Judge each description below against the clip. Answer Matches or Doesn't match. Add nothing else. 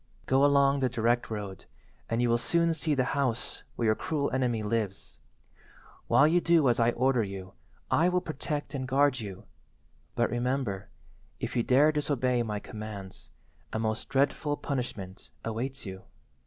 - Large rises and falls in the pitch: Doesn't match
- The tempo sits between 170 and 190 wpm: Doesn't match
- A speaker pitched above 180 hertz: Doesn't match